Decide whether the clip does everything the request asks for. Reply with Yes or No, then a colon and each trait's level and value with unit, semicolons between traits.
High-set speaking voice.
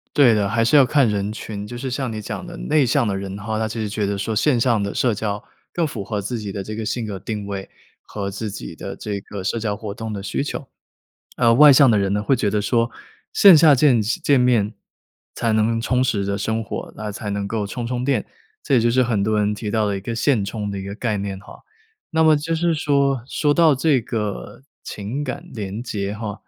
No: low, 110 Hz